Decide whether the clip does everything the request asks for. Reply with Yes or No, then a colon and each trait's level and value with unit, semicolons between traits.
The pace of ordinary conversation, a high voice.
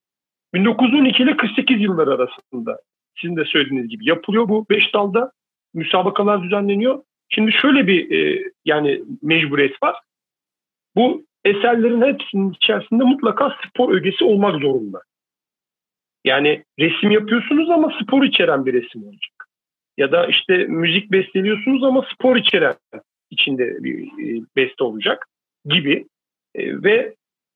Yes: average, 115 wpm; high, 220 Hz